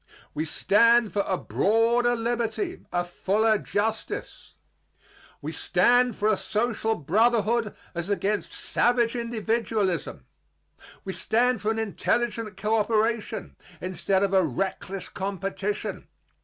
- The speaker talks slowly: Yes, slow, 110 wpm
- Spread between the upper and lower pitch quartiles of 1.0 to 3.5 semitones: Yes, average, 3.1 semitones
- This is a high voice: Yes, high, 215 Hz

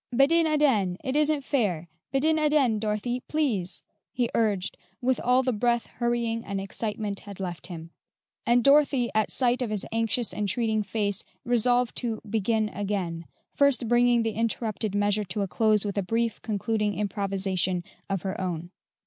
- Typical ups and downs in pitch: Yes, average, 3.5 semitones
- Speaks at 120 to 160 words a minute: Yes, average, 155 wpm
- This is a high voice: Yes, high, 220 Hz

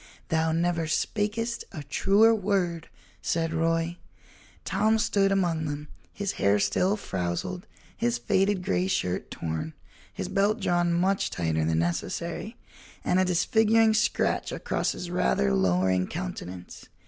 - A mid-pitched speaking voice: Yes, medium, 170 Hz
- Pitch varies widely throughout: Yes, wide, 8.8 semitones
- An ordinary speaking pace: No, slow, 130 wpm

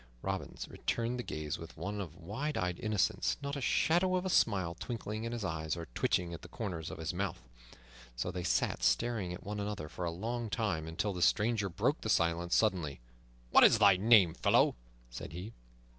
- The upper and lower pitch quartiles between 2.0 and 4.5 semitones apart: No, average, 4.9 semitones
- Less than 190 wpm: No, average, 200 wpm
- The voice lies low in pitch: Yes, very low, 95 Hz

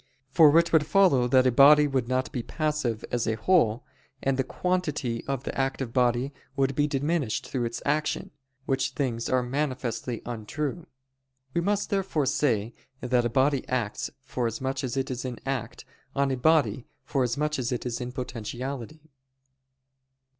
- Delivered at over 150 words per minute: Yes, average, 160 wpm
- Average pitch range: Yes, average, 3.4 semitones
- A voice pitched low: Yes, low, 130 Hz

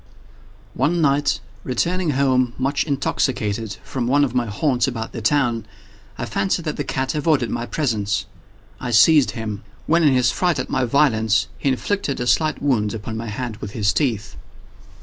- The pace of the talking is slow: No, average, 170 wpm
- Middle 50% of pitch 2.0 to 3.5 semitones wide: No, average, 4.5 semitones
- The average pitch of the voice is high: No, low, 130 Hz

